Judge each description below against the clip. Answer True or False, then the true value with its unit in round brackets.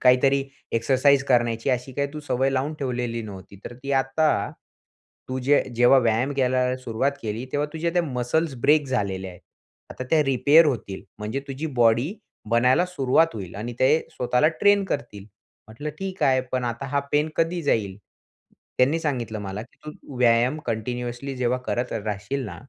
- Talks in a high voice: False (130 Hz)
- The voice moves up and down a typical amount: True (3.4 semitones)